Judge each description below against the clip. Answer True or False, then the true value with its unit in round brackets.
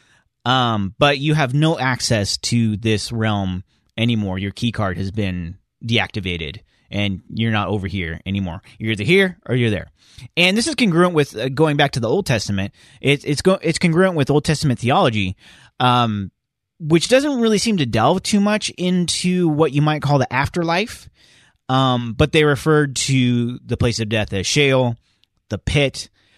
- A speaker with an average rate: True (175 wpm)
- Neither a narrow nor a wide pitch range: False (6.8 semitones)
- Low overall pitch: True (125 Hz)